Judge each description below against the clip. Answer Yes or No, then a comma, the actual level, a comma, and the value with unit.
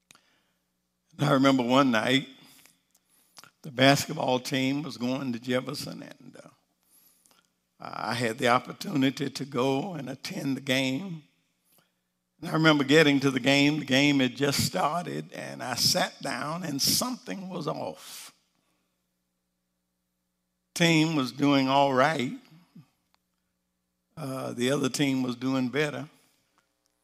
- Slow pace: Yes, slow, 120 wpm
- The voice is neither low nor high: No, low, 130 Hz